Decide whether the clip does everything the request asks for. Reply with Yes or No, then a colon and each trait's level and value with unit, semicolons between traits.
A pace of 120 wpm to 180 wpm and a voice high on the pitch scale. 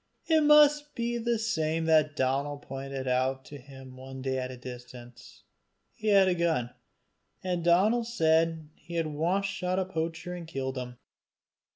No: average, 165 wpm; medium, 160 Hz